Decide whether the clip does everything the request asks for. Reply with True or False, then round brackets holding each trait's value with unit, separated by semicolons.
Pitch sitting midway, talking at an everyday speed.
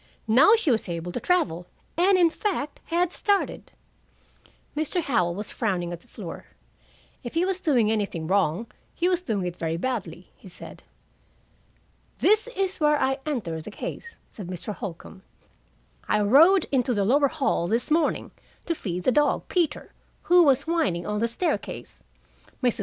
False (250 Hz; 165 wpm)